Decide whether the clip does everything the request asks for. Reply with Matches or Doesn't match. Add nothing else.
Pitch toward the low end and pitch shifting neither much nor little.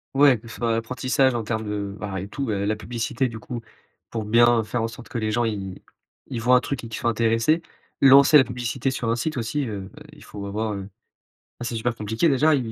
Matches